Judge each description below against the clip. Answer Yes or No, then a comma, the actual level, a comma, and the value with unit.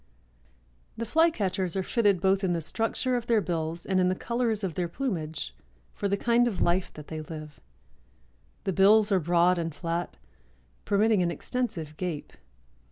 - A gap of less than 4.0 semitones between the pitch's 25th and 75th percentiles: No, average, 4.5 semitones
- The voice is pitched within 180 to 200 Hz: Yes, medium, 185 Hz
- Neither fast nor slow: Yes, average, 170 wpm